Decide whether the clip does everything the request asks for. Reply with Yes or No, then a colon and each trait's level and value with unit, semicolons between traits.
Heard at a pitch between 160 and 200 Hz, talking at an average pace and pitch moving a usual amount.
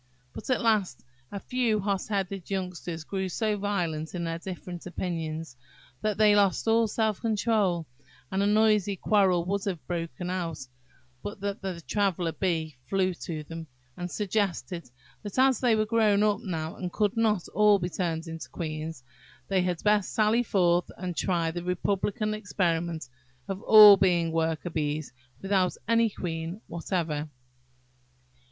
Yes: medium, 185 Hz; average, 155 wpm; average, 3.8 semitones